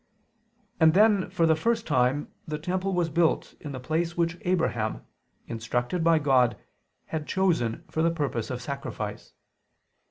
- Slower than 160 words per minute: Yes, average, 150 wpm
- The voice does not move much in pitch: No, average, 5.0 semitones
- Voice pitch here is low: No, medium, 160 Hz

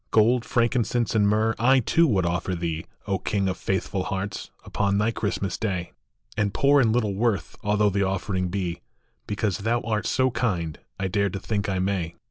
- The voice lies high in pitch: No, low, 100 Hz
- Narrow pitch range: No, average, 3.0 semitones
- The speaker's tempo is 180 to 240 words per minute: Yes, average, 185 wpm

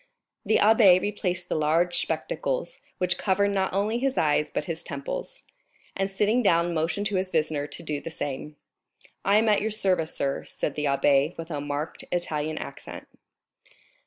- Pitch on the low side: No, medium, 175 Hz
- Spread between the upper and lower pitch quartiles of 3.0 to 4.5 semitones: No, average, 4.9 semitones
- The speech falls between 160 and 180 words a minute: Yes, average, 170 wpm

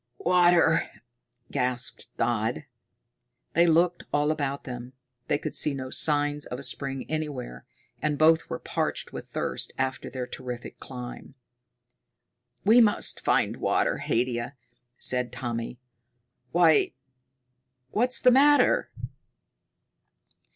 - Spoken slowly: Yes, slow, 110 wpm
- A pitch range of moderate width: Yes, average, 4.6 semitones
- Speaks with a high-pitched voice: No, medium, 140 Hz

